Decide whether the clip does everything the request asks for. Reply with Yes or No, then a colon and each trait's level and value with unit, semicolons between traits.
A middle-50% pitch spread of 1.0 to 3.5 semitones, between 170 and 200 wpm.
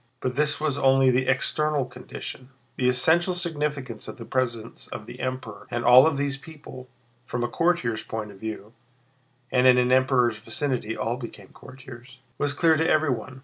Yes: average, 3.2 semitones; average, 175 wpm